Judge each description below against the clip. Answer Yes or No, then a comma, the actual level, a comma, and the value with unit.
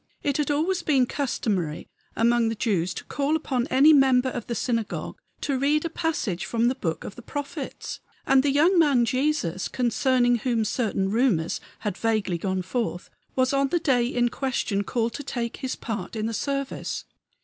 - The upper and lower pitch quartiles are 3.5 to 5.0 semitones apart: Yes, average, 3.8 semitones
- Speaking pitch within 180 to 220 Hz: No, high, 245 Hz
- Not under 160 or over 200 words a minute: Yes, average, 180 wpm